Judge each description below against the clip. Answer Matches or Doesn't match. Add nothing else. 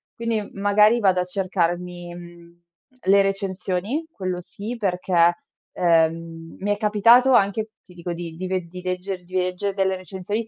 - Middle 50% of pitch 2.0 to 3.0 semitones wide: Matches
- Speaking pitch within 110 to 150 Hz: Doesn't match